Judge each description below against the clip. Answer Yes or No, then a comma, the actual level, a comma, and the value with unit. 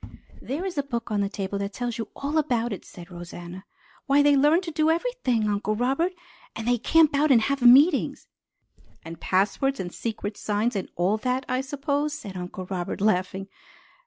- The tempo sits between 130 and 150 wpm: No, average, 190 wpm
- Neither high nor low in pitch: No, high, 240 Hz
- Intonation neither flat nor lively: No, wide, 6.1 semitones